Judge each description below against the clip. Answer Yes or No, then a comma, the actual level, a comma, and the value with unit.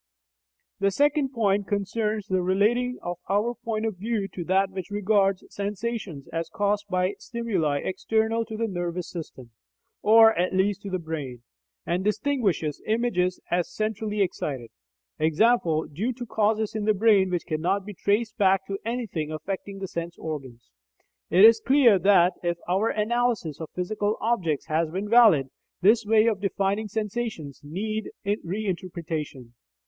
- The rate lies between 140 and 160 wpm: Yes, average, 150 wpm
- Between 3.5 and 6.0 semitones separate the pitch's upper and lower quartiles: Yes, average, 3.9 semitones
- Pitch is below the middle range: No, high, 200 Hz